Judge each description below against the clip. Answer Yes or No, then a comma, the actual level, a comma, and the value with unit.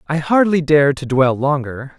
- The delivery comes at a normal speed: Yes, average, 180 wpm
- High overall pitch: No, medium, 145 Hz